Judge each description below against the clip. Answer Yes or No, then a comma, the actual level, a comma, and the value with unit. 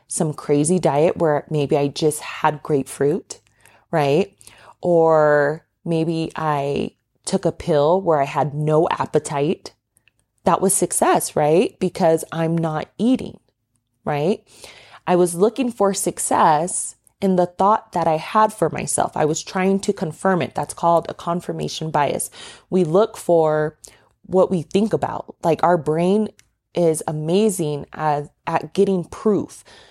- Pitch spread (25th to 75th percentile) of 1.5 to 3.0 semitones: No, average, 3.7 semitones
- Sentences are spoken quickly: No, average, 140 wpm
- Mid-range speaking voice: Yes, medium, 165 Hz